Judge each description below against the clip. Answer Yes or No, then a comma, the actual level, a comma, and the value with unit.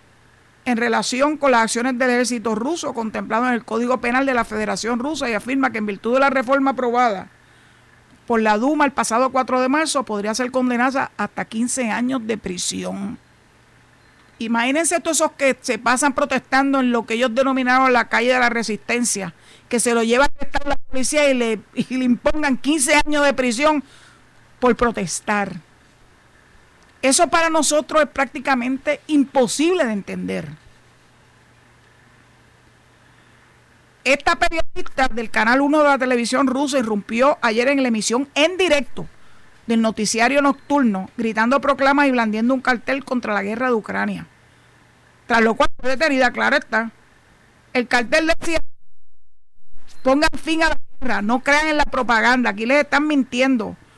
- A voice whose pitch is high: Yes, very high, 255 Hz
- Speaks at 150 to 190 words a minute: Yes, average, 155 wpm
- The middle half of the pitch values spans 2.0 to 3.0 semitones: No, average, 4.0 semitones